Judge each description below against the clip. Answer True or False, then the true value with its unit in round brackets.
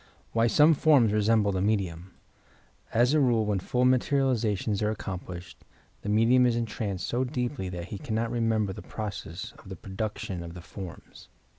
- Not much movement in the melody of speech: False (4.1 semitones)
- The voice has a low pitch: True (110 Hz)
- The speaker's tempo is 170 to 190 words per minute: True (180 wpm)